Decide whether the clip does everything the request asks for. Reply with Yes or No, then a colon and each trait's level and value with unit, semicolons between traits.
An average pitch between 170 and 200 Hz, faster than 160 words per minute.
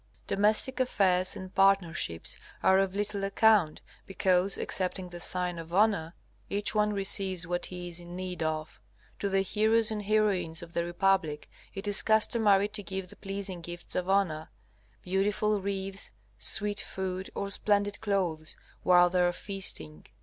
No: high, 190 Hz; average, 155 wpm